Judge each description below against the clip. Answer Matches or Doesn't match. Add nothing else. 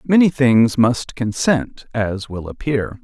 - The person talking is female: Doesn't match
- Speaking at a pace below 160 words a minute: Matches